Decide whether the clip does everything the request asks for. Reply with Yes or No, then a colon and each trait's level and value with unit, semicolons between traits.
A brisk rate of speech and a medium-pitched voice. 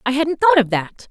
No: fast, 270 wpm; very high, 275 Hz